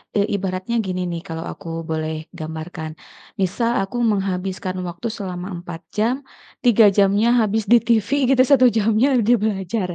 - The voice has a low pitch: No, high, 195 Hz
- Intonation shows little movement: No, average, 3.8 semitones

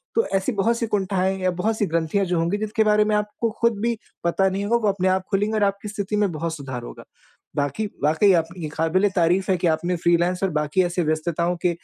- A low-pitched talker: No, medium, 185 Hz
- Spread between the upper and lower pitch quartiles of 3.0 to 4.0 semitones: Yes, average, 3.7 semitones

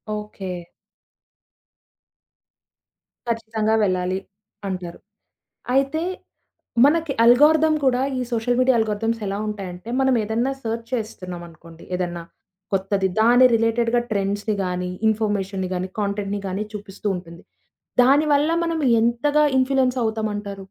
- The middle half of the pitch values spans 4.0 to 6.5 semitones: Yes, average, 4.3 semitones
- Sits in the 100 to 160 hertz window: No, high, 220 Hz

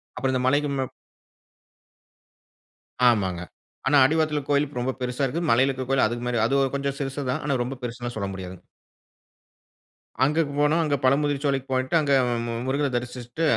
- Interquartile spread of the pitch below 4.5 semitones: Yes, average, 2.9 semitones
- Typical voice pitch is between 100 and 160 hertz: Yes, low, 135 Hz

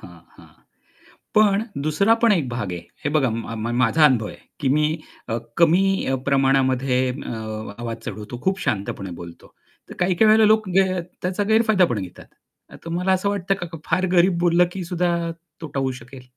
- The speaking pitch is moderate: Yes, medium, 165 Hz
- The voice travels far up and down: Yes, wide, 6.9 semitones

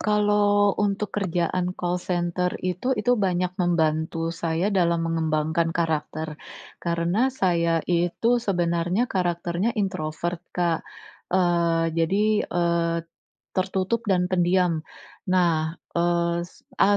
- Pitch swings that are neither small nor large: No, narrow, 2.3 semitones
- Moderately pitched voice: Yes, medium, 175 Hz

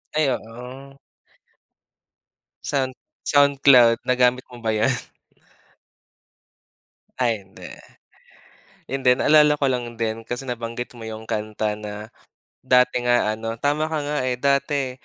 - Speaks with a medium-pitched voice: No, low, 125 Hz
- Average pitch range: Yes, average, 3.4 semitones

